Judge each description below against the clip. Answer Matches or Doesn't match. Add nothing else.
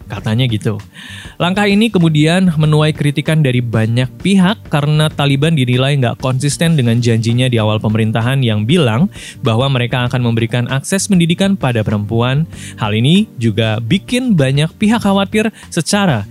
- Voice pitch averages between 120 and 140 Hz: Matches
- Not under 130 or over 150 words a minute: Matches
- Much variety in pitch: Matches